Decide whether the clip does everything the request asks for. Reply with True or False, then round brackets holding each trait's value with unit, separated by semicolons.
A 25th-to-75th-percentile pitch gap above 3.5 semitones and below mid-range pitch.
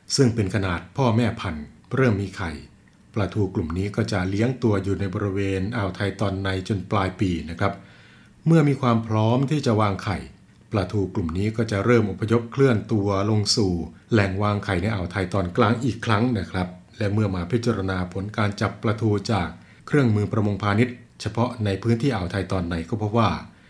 False (3.2 semitones; 105 Hz)